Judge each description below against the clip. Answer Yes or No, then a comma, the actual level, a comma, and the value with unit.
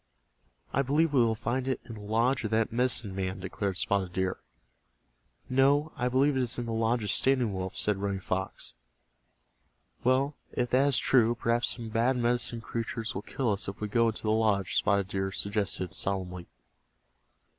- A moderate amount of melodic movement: Yes, average, 3.9 semitones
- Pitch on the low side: Yes, low, 115 Hz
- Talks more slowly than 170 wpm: No, average, 180 wpm